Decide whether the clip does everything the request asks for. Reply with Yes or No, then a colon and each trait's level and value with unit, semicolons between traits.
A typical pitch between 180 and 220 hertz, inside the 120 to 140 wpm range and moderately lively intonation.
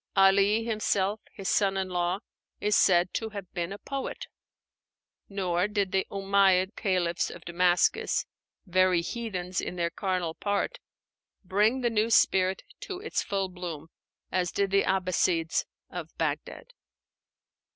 No: high, 190 Hz; slow, 135 wpm; narrow, 2.2 semitones